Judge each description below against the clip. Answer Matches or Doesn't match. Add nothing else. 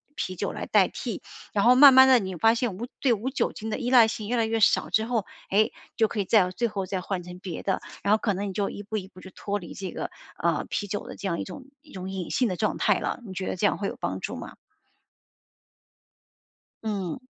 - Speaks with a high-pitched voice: Matches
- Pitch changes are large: Doesn't match